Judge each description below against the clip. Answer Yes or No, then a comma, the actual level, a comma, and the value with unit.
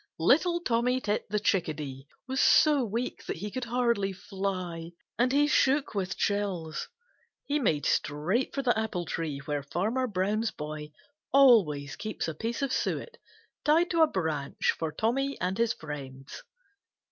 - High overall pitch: Yes, high, 205 Hz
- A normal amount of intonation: No, wide, 7.8 semitones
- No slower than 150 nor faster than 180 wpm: Yes, average, 155 wpm